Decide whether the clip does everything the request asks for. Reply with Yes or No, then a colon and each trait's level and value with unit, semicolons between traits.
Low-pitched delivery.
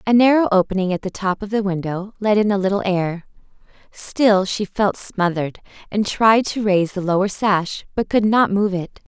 No: high, 200 Hz